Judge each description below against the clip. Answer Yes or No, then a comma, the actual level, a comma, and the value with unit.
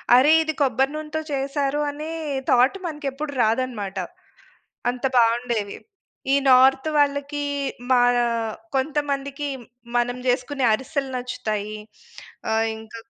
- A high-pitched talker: Yes, very high, 265 Hz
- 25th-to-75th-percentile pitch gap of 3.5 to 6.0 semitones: No, average, 2.9 semitones